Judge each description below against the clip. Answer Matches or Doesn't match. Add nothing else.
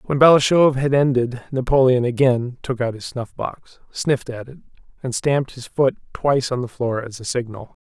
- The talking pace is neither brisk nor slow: Matches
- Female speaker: Doesn't match